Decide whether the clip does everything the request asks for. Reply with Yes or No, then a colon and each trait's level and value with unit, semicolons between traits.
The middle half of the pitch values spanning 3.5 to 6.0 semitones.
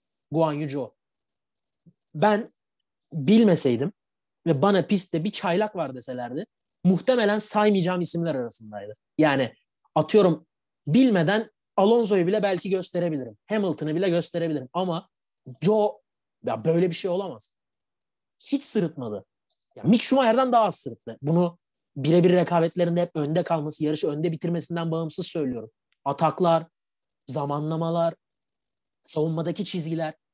Yes: average, 3.8 semitones